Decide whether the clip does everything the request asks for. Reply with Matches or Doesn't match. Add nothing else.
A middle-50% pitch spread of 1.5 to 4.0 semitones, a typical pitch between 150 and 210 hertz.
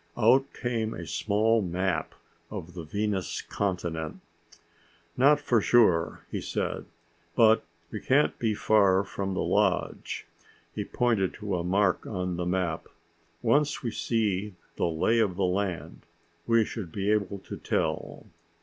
Doesn't match